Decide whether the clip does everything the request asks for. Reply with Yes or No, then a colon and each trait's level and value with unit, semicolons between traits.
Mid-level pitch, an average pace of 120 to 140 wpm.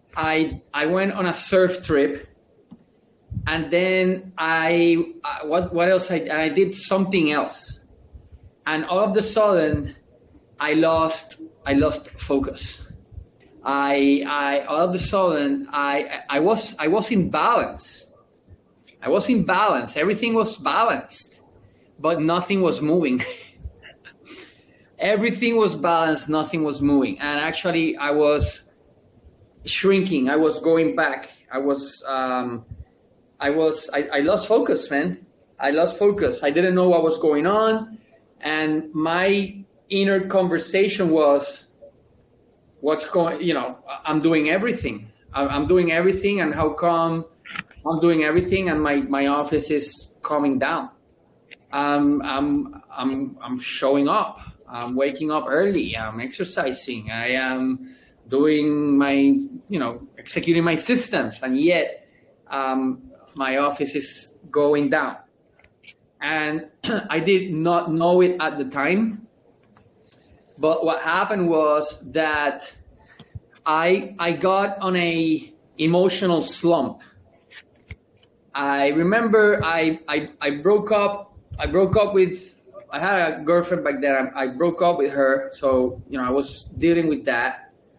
Yes: medium, 160 Hz; slow, 135 wpm